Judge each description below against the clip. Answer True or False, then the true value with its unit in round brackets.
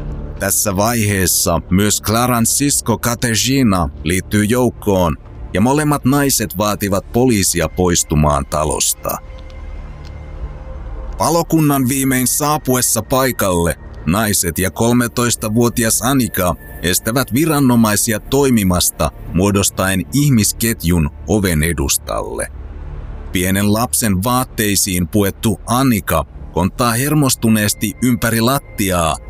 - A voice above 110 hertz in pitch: False (105 Hz)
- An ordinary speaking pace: False (80 wpm)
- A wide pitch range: True (6.1 semitones)